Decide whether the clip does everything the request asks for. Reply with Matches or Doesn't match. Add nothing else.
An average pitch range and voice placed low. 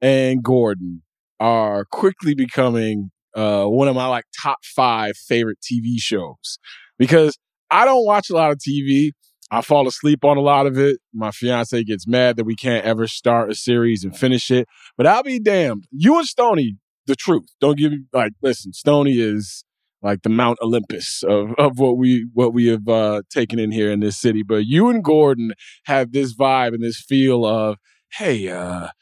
Matches